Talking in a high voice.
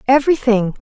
Yes: high, 245 Hz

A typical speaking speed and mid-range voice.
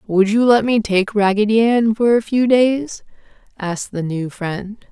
No: average, 185 wpm; high, 215 Hz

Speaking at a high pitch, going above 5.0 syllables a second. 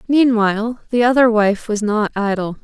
No: high, 220 Hz; 4.8 syllables/s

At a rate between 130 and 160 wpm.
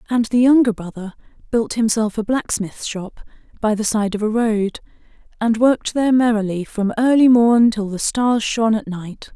No: average, 180 wpm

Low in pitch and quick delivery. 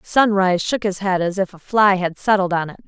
No: high, 190 Hz; fast, 250 wpm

